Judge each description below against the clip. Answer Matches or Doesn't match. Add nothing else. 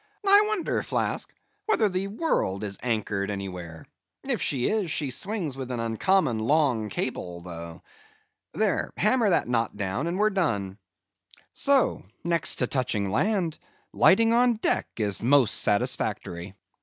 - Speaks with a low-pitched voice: Matches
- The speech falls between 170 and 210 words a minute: Doesn't match